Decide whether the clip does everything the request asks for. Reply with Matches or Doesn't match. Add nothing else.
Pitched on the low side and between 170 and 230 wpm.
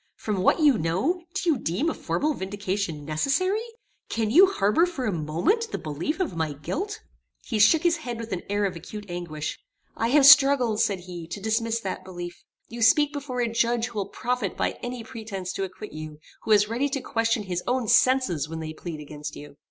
Doesn't match